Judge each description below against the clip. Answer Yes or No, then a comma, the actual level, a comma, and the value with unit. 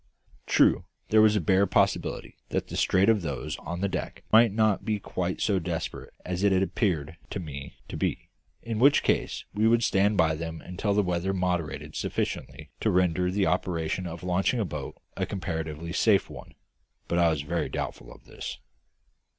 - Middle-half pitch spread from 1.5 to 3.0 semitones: No, average, 3.5 semitones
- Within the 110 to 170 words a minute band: No, average, 185 wpm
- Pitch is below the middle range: Yes, very low, 90 Hz